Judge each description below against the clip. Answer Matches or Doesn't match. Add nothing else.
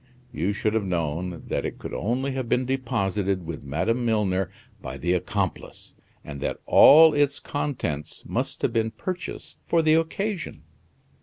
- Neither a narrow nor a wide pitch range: Doesn't match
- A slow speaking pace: Doesn't match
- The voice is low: Matches